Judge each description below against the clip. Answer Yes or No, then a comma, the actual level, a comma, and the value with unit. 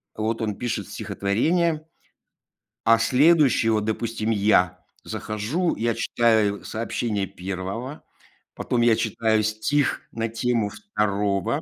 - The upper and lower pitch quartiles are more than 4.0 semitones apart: No, average, 2.9 semitones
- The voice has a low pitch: Yes, low, 110 Hz